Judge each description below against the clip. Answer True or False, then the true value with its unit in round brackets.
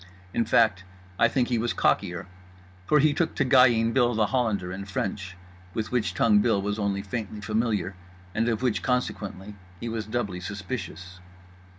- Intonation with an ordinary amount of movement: True (3.4 semitones)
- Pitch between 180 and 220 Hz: False (110 Hz)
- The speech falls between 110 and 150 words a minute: False (170 wpm)